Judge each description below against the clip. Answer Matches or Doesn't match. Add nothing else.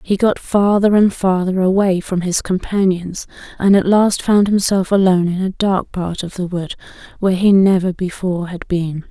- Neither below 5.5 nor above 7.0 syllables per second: Doesn't match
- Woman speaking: Matches